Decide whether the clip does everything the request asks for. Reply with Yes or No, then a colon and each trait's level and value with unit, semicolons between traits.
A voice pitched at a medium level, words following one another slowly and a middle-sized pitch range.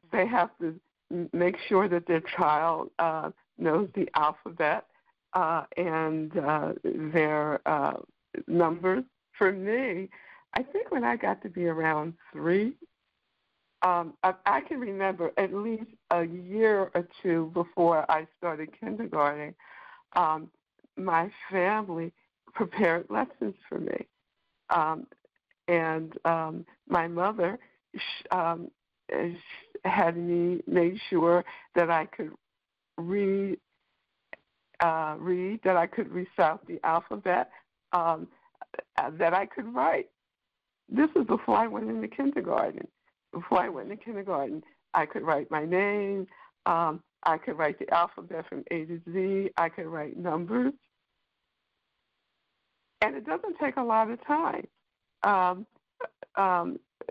Yes: medium, 175 Hz; slow, 125 wpm; average, 3.6 semitones